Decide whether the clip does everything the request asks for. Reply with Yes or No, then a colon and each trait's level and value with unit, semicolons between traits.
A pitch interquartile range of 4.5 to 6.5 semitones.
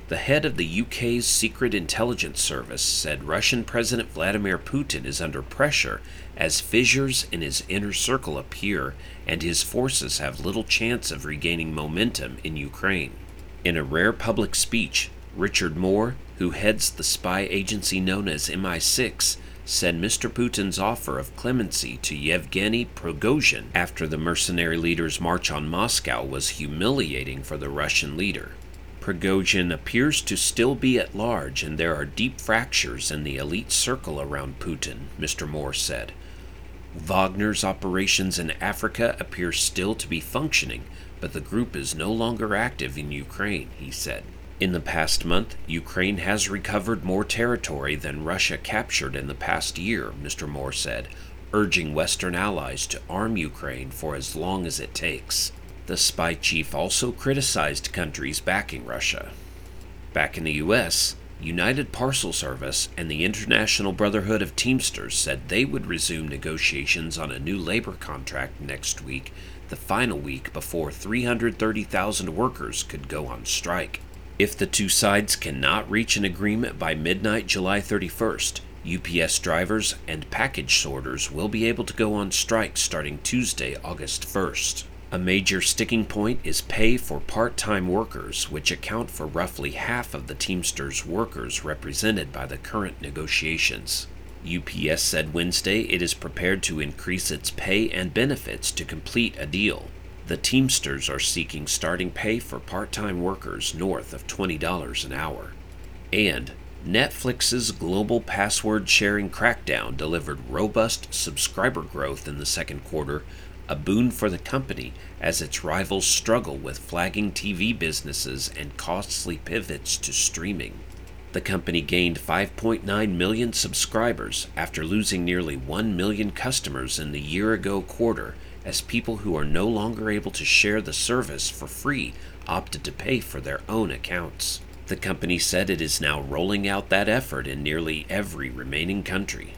Yes: average, 5.1 semitones